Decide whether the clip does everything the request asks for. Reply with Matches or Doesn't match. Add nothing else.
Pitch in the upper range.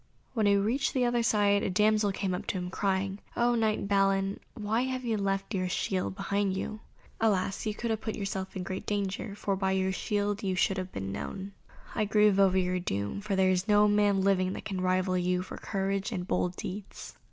Matches